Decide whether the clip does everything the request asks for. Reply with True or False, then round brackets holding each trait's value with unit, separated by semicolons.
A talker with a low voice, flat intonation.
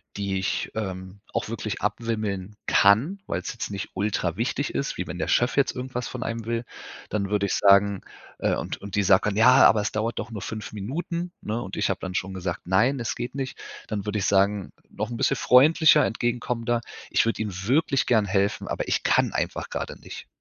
False (110 Hz; 3.4 semitones)